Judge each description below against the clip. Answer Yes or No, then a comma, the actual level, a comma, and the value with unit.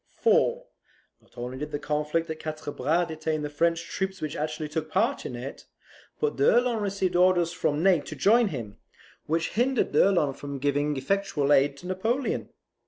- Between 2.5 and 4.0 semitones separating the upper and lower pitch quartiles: No, average, 4.7 semitones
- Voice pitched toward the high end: No, medium, 160 Hz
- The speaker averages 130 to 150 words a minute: No, average, 170 wpm